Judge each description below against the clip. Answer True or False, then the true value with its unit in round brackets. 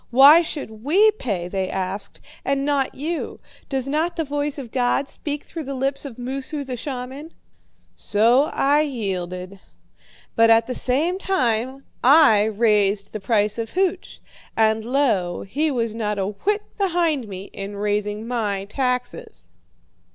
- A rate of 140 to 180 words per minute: True (150 wpm)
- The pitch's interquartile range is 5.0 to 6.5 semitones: True (5.6 semitones)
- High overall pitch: True (250 Hz)